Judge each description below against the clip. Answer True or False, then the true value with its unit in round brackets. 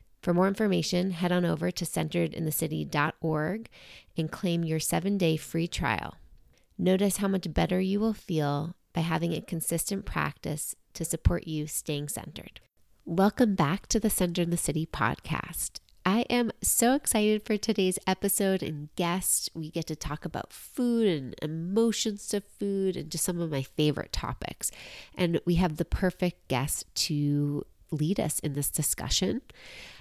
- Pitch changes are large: False (3.8 semitones)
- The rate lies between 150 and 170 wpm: True (160 wpm)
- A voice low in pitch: False (175 Hz)